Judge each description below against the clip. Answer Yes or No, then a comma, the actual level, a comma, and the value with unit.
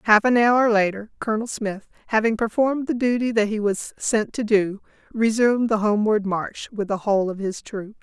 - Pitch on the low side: No, high, 215 Hz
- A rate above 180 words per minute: Yes, average, 195 wpm